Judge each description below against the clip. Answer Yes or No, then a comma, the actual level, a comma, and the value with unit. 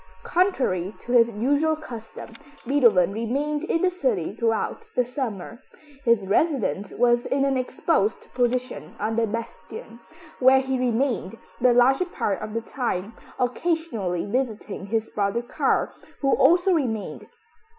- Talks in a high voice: Yes, high, 240 Hz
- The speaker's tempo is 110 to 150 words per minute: Yes, slow, 135 wpm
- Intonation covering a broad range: No, average, 3.8 semitones